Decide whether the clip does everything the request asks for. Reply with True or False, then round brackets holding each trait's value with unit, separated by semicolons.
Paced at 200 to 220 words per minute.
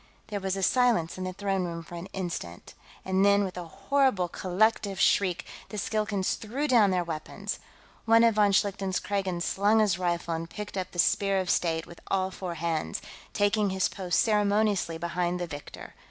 False (185 wpm)